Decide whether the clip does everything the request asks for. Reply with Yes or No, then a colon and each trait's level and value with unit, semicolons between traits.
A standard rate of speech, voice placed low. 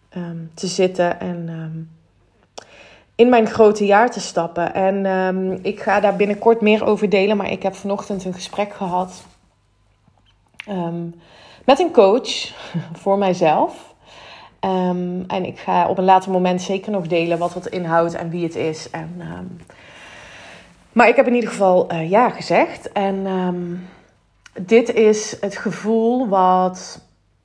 No: average, 150 wpm; medium, 185 Hz